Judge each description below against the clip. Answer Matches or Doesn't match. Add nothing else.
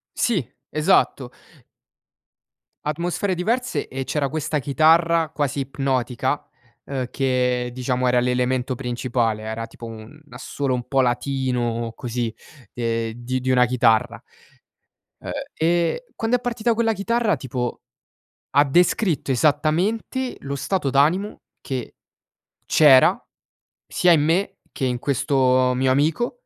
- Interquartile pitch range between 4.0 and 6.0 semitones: Matches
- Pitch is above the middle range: Doesn't match